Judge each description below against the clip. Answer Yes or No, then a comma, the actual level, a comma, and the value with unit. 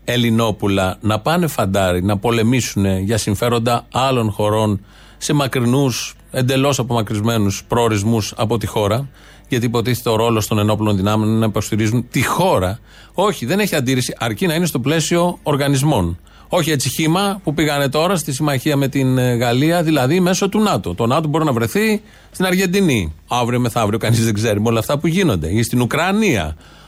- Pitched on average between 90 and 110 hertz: No, low, 120 Hz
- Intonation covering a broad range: Yes, wide, 5.8 semitones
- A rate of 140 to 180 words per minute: Yes, average, 165 wpm